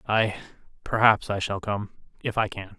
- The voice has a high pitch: No, low, 100 Hz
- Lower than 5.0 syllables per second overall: Yes, 4.8 syllables/s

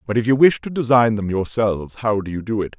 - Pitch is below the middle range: Yes, low, 115 Hz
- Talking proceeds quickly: Yes, fast, 280 wpm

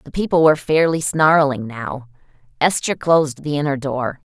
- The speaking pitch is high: No, medium, 145 Hz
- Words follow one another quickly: No, average, 155 wpm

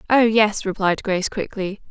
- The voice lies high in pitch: Yes, high, 205 Hz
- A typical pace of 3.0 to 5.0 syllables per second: Yes, 4.9 syllables/s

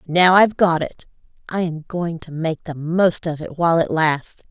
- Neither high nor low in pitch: Yes, medium, 165 Hz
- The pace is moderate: No, fast, 225 wpm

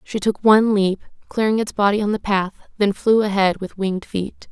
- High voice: Yes, high, 205 Hz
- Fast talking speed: Yes, fast, 210 wpm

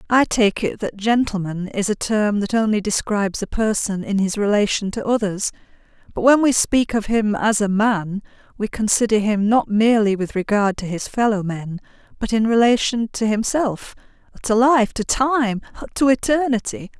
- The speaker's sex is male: No, female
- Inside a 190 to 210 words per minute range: No, average, 160 wpm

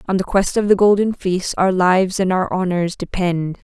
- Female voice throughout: Yes, female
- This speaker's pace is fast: Yes, fast, 210 wpm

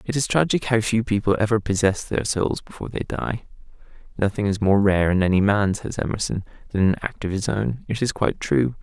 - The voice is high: No, low, 105 Hz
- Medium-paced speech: No, fast, 220 wpm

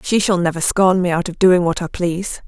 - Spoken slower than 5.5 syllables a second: No, 5.6 syllables/s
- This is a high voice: No, medium, 180 Hz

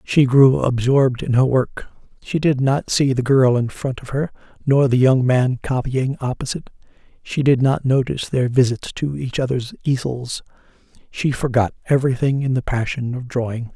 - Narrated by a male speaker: Yes, male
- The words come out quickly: No, average, 175 wpm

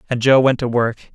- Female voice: No, male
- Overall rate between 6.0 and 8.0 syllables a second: Yes, 6.3 syllables/s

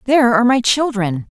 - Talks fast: No, average, 180 wpm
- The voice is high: Yes, high, 235 Hz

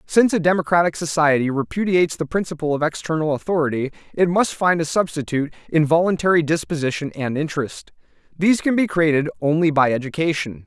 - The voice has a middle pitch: Yes, medium, 160 Hz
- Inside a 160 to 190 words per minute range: No, average, 150 wpm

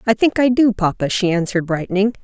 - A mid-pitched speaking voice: No, high, 205 Hz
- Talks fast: Yes, fast, 215 wpm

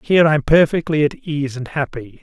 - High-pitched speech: No, medium, 145 Hz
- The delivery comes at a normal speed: Yes, average, 190 wpm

